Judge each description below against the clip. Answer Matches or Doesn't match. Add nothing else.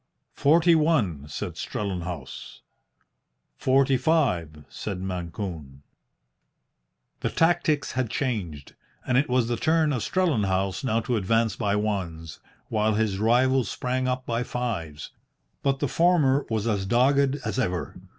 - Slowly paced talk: Matches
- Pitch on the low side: Matches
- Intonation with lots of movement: Matches